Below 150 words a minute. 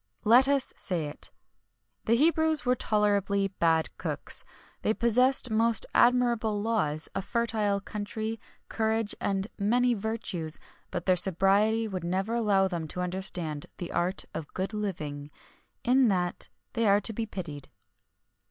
Yes: average, 140 wpm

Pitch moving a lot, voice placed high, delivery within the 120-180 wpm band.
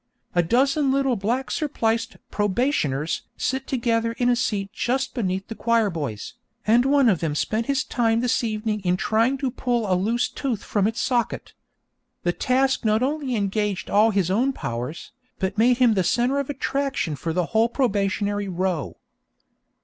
No: average, 4.5 semitones; high, 225 Hz; average, 170 wpm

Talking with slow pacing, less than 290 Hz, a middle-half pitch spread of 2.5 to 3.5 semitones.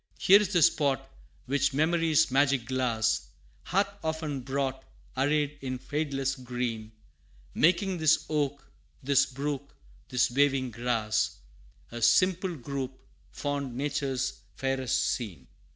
Yes: slow, 115 wpm; low, 135 Hz; average, 2.9 semitones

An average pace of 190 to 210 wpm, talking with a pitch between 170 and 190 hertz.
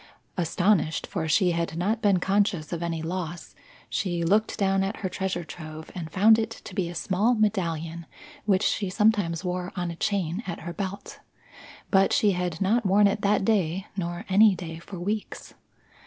No: average, 180 wpm; medium, 185 Hz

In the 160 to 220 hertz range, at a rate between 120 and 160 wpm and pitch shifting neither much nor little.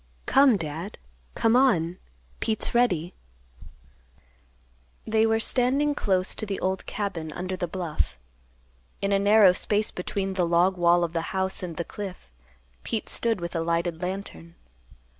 Yes: high, 190 Hz; average, 145 wpm; average, 4.0 semitones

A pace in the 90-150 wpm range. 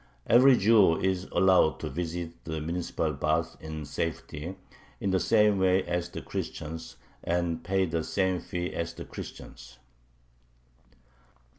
Yes: slow, 135 wpm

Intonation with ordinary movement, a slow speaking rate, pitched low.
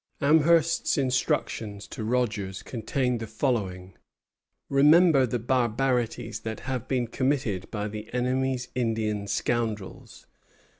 Yes: average, 3.6 semitones; slow, 105 wpm; low, 120 Hz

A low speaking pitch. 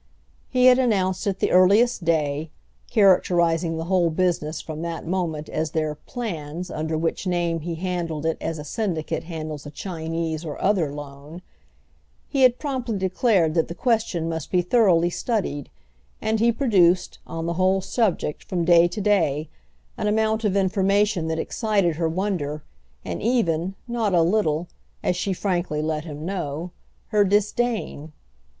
No: medium, 175 Hz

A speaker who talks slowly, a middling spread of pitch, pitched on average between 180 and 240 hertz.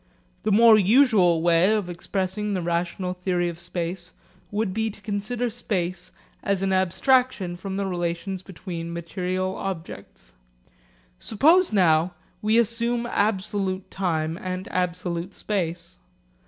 Yes: slow, 125 wpm; average, 3.1 semitones; medium, 185 Hz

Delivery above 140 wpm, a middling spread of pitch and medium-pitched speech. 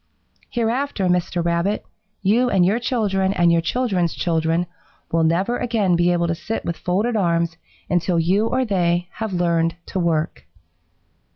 Yes: average, 155 wpm; average, 4.0 semitones; medium, 180 Hz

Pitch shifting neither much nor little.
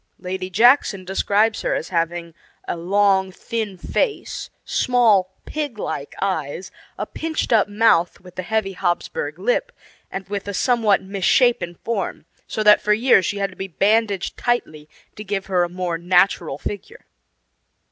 Yes: average, 3.5 semitones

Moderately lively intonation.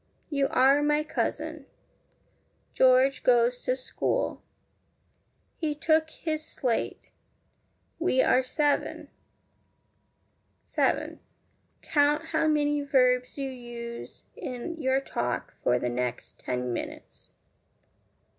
Yes: average, 3.2 semitones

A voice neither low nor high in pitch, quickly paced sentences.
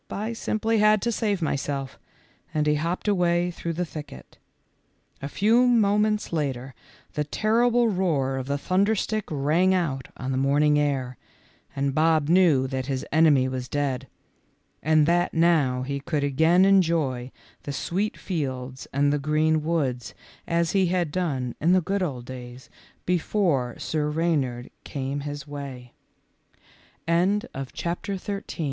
No: medium, 155 Hz; slow, 135 wpm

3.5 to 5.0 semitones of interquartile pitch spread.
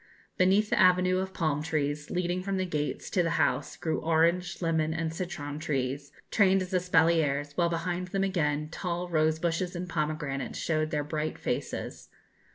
No: average, 3.0 semitones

